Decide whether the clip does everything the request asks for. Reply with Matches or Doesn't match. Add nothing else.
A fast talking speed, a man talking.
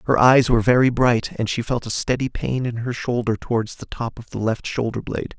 Matches